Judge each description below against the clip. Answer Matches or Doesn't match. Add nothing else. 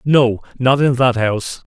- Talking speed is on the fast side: Doesn't match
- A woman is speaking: Doesn't match